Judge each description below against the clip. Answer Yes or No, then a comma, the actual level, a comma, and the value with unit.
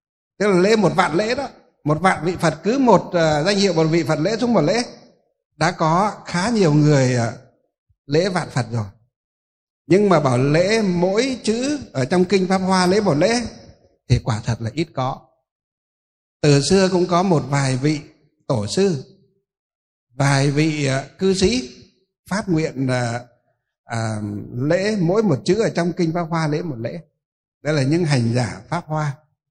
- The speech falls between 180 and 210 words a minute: Yes, average, 185 wpm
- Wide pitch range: Yes, wide, 6.3 semitones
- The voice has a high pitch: No, medium, 155 Hz